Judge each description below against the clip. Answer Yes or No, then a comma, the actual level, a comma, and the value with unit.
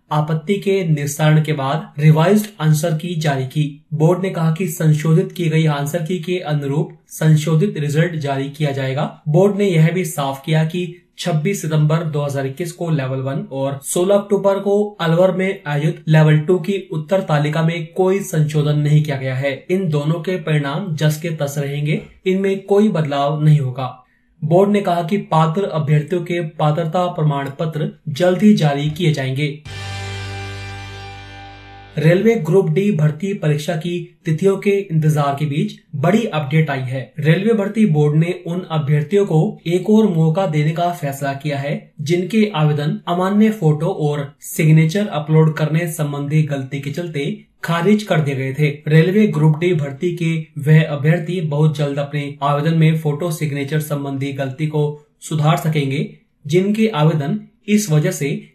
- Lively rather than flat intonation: No, average, 3.7 semitones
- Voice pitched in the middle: Yes, medium, 160 Hz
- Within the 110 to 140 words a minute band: No, average, 160 wpm